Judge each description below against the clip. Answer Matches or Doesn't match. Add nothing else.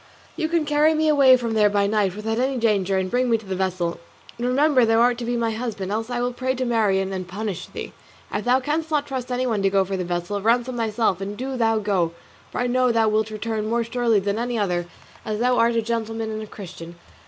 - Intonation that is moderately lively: Matches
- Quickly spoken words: Matches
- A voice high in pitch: Matches